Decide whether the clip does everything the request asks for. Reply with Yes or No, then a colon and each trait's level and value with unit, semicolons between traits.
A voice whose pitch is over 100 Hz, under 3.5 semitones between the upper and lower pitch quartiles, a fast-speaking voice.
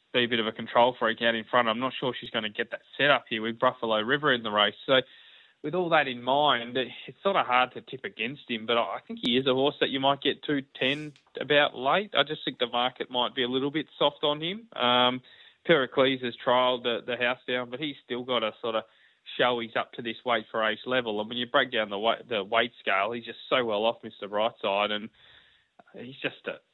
Yes: low, 125 Hz; average, 2.8 semitones; fast, 255 wpm